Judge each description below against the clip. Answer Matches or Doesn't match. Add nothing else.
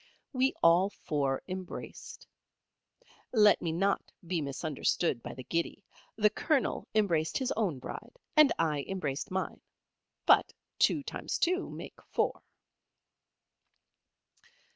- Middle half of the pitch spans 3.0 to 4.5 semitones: Doesn't match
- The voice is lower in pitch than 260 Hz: Matches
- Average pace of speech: Doesn't match